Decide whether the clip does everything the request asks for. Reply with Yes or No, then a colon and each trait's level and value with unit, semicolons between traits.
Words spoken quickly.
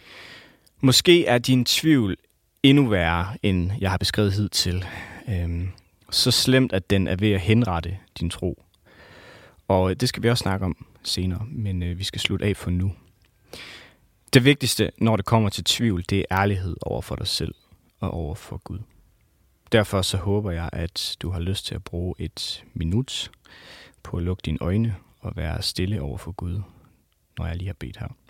No: average, 180 wpm